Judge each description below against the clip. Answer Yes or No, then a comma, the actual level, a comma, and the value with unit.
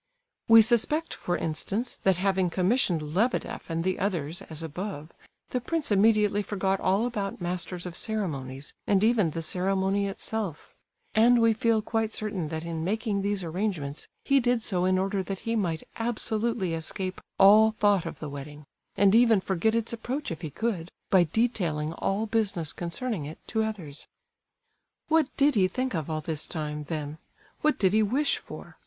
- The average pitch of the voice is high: Yes, high, 195 Hz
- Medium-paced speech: Yes, average, 170 wpm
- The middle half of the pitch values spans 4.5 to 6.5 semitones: Yes, average, 5.0 semitones